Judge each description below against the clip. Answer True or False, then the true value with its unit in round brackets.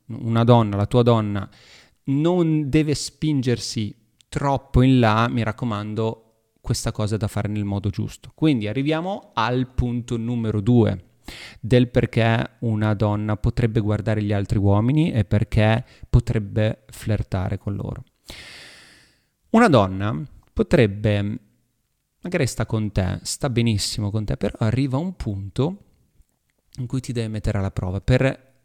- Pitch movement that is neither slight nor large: True (3.2 semitones)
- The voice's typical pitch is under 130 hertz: True (115 Hz)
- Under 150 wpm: True (140 wpm)